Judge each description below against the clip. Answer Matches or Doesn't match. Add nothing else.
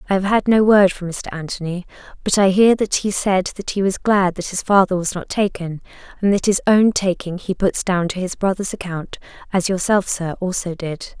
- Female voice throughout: Matches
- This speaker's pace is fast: Matches